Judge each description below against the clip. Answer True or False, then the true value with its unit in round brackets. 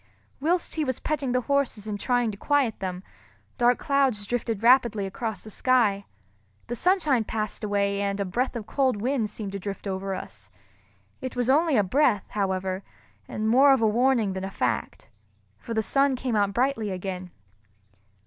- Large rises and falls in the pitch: False (4.6 semitones)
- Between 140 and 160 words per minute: False (175 wpm)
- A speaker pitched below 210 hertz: False (220 Hz)